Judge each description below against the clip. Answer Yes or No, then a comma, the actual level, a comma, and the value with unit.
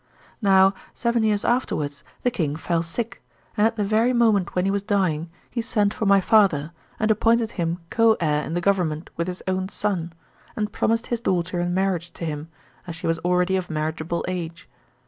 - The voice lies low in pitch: No, medium, 185 Hz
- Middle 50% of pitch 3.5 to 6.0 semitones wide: Yes, average, 4.3 semitones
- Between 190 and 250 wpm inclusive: Yes, average, 195 wpm